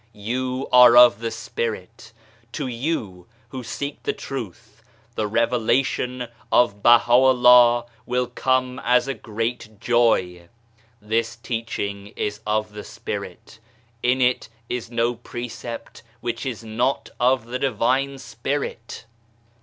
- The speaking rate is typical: No, slow, 120 wpm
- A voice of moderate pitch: No, low, 120 Hz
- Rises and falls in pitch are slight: Yes, narrow, 2.1 semitones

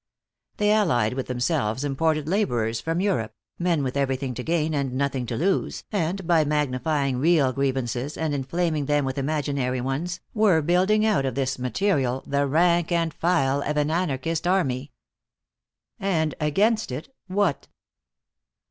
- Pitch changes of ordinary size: Yes, average, 4.6 semitones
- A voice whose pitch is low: No, medium, 150 Hz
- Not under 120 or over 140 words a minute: No, average, 150 wpm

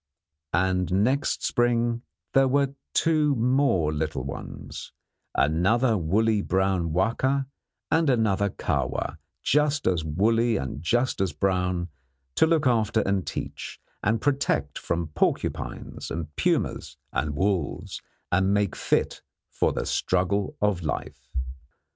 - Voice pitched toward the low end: Yes, low, 100 Hz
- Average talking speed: No, slow, 120 wpm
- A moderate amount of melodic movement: No, wide, 5.7 semitones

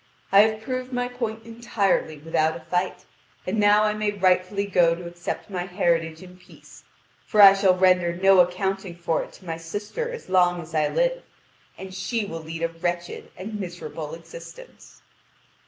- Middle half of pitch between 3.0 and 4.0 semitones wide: Yes, average, 3.5 semitones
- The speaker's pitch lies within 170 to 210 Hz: Yes, medium, 185 Hz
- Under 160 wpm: No, average, 175 wpm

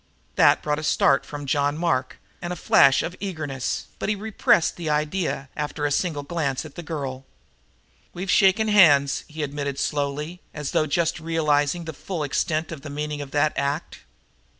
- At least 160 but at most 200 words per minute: Yes, average, 175 wpm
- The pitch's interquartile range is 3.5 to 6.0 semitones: No, average, 3.1 semitones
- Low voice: No, medium, 150 Hz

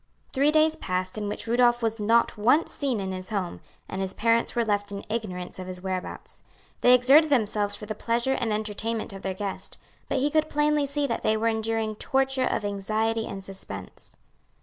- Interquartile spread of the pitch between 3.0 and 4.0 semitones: Yes, average, 3.7 semitones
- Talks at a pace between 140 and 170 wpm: No, average, 195 wpm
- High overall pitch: Yes, high, 220 Hz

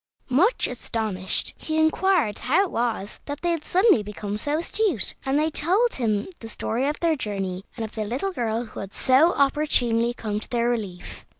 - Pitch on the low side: No, high, 245 Hz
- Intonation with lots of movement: Yes, wide, 6.6 semitones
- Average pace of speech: Yes, average, 190 wpm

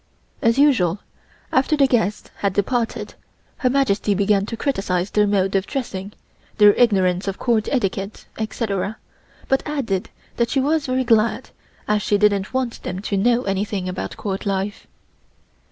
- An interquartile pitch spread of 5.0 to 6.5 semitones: No, average, 3.9 semitones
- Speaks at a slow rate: No, average, 155 wpm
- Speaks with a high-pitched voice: Yes, high, 210 Hz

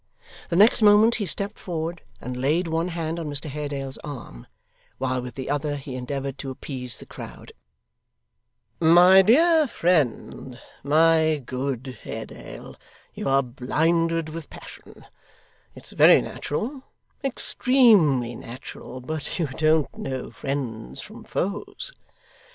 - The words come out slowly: Yes, slow, 125 wpm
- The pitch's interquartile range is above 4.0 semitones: Yes, average, 4.6 semitones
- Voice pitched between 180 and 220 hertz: No, medium, 150 Hz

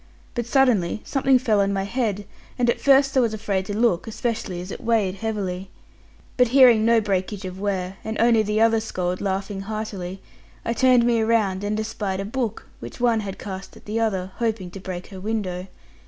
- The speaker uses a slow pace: No, average, 200 wpm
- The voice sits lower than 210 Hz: No, high, 215 Hz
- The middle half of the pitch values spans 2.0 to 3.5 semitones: Yes, average, 3.2 semitones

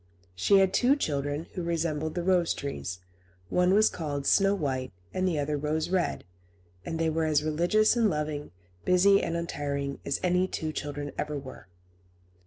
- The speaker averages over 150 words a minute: Yes, average, 170 wpm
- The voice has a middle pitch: Yes, medium, 160 Hz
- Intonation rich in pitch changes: No, average, 3.9 semitones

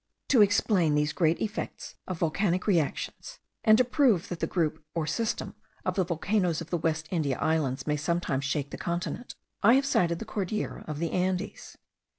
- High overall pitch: No, medium, 170 Hz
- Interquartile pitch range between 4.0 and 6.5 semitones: Yes, average, 4.5 semitones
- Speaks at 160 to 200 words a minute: Yes, average, 180 wpm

